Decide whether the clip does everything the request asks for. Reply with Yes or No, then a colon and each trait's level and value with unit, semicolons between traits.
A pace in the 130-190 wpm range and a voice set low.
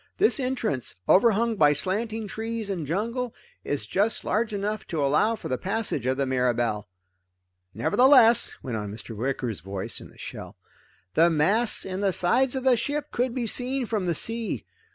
No: average, 175 wpm; high, 205 Hz